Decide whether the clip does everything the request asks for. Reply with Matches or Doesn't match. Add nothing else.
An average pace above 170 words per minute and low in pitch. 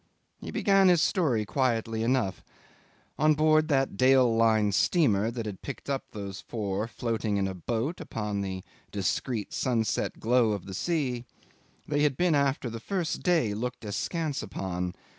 Doesn't match